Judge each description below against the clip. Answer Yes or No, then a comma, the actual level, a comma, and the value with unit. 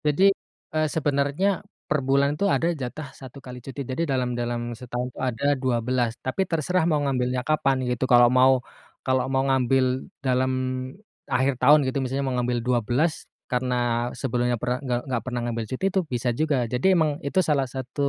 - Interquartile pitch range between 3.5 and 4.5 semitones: No, narrow, 2.5 semitones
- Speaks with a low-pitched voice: Yes, low, 130 Hz